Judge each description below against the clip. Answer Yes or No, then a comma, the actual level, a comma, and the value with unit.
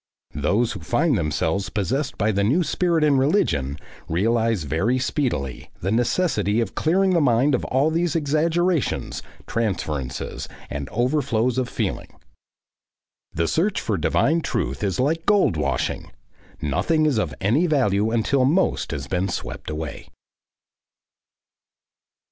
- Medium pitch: No, low, 115 Hz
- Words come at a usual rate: No, slow, 130 wpm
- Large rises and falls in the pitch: Yes, wide, 8.8 semitones